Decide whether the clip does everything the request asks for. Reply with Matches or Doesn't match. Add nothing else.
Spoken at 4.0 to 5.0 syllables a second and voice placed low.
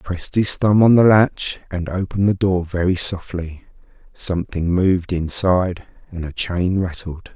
Matches